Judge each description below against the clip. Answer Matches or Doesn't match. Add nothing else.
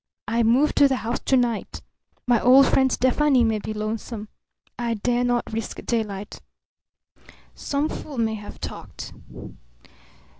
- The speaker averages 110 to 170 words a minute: Matches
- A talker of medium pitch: Doesn't match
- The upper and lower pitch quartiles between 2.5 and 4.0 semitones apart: Matches